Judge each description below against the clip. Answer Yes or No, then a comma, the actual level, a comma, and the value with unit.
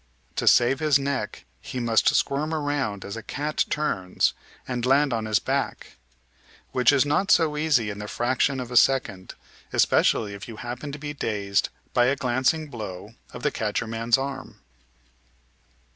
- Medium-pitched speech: No, low, 125 Hz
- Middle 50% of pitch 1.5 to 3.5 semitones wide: No, average, 4.4 semitones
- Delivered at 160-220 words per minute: Yes, average, 165 wpm